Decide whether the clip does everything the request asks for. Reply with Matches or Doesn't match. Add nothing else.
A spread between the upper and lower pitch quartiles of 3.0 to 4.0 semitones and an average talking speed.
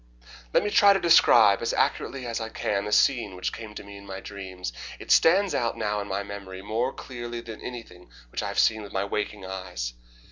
Doesn't match